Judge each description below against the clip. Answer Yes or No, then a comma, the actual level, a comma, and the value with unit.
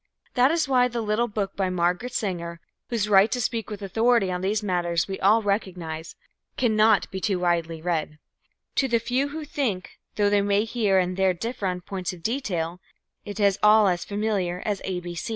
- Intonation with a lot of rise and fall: No, average, 3.7 semitones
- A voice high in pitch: Yes, high, 200 Hz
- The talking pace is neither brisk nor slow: Yes, average, 190 wpm